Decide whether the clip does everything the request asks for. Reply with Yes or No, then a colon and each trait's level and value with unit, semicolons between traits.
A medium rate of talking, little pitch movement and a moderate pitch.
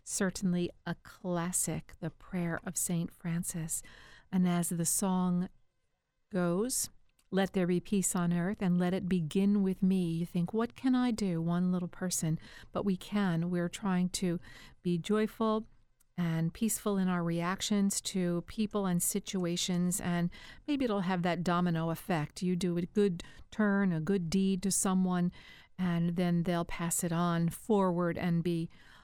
Yes: average, 160 wpm; narrow, 2.0 semitones; medium, 180 Hz